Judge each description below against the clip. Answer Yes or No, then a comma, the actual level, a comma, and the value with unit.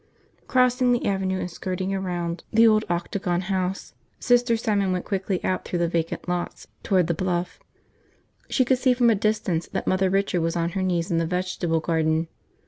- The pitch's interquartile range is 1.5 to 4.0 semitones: Yes, average, 3.2 semitones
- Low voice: No, medium, 185 Hz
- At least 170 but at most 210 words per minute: Yes, average, 185 wpm